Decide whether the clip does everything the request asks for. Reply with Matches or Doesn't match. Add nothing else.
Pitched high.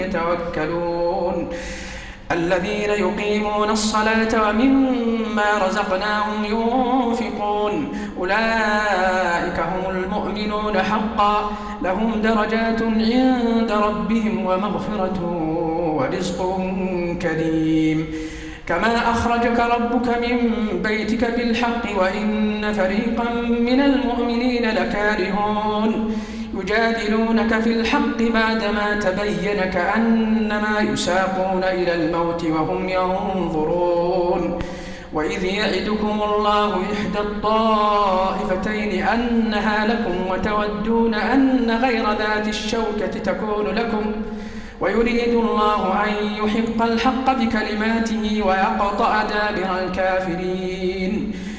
Matches